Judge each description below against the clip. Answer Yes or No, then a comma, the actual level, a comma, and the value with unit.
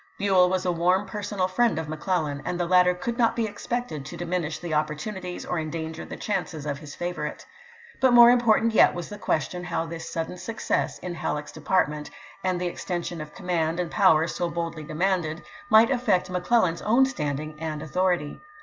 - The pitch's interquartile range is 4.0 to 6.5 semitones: No, average, 3.4 semitones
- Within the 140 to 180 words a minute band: No, average, 190 wpm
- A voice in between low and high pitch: Yes, medium, 175 Hz